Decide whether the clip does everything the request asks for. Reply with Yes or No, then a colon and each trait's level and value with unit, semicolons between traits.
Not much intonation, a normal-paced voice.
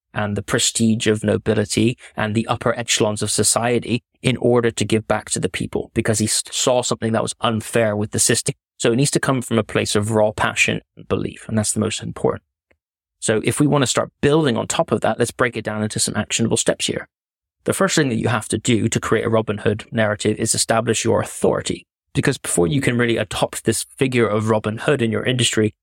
No: narrow, 2.1 semitones; fast, 230 wpm